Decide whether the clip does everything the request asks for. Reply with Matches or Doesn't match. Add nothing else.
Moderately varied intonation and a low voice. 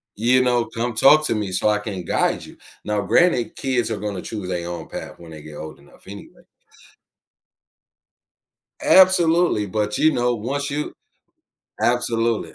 Matches